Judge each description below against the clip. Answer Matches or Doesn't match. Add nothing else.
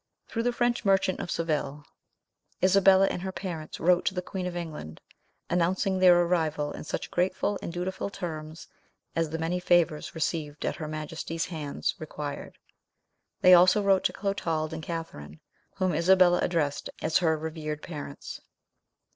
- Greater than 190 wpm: Doesn't match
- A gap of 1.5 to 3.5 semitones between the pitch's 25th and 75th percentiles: Matches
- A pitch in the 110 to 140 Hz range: Doesn't match